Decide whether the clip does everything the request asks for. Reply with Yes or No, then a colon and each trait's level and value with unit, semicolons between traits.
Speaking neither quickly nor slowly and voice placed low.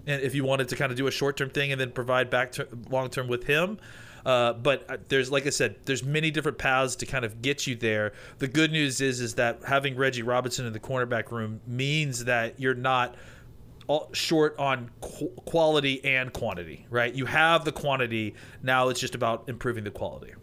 No: fast, 210 wpm; low, 130 Hz